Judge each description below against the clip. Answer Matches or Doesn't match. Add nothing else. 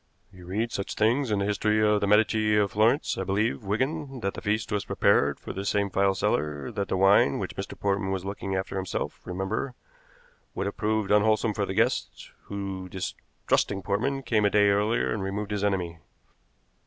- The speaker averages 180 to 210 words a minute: Matches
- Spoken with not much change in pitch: Matches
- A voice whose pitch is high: Doesn't match